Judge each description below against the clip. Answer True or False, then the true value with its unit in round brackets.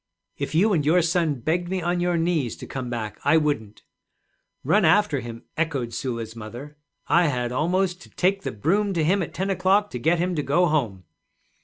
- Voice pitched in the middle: True (160 Hz)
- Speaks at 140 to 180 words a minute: False (200 wpm)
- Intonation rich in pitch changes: True (6.2 semitones)